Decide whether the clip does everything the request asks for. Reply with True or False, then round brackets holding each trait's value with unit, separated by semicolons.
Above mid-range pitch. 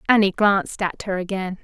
True (195 Hz)